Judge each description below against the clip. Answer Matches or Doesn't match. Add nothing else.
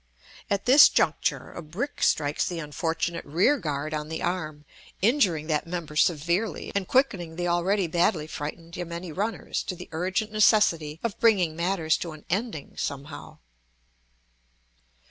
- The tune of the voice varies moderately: Matches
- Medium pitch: Matches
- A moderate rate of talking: Matches